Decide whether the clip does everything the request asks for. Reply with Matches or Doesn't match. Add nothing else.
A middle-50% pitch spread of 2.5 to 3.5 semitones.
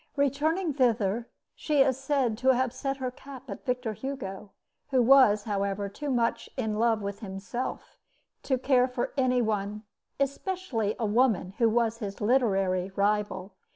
Doesn't match